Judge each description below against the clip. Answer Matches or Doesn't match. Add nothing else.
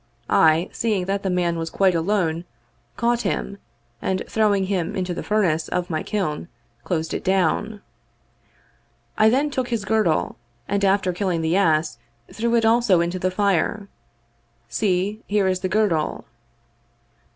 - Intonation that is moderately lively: Matches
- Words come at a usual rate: Matches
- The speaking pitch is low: Doesn't match